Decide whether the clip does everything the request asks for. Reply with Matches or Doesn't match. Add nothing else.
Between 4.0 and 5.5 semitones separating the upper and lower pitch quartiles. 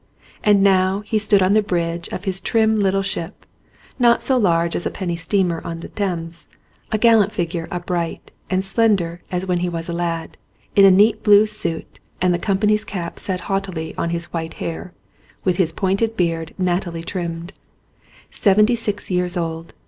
Doesn't match